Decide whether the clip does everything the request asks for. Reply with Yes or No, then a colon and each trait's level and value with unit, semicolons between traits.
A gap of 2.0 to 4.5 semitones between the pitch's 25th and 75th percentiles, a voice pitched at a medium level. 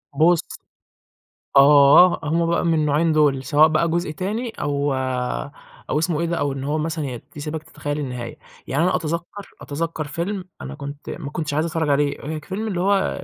Yes: average, 2.8 semitones; medium, 155 Hz